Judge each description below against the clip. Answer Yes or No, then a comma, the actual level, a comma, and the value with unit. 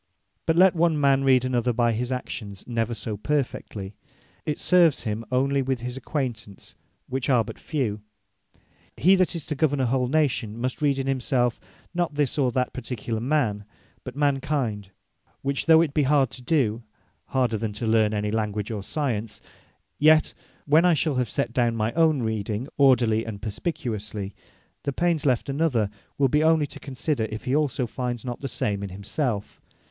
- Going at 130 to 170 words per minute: No, average, 180 wpm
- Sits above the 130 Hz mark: No, low, 125 Hz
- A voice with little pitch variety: No, average, 4.6 semitones